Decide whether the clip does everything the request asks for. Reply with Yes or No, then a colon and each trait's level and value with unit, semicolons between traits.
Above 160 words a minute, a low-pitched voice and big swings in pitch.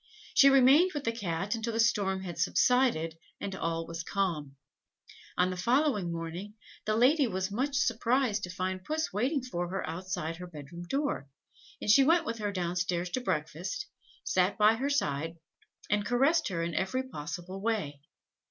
No: average, 175 wpm; high, 195 Hz; wide, 6.4 semitones